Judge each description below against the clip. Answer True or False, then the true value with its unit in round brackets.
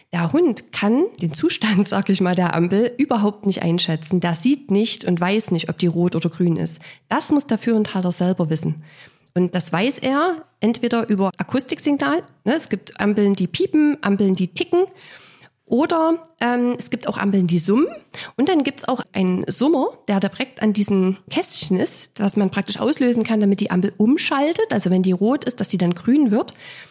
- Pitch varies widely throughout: True (6.1 semitones)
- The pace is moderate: False (195 wpm)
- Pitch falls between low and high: False (205 Hz)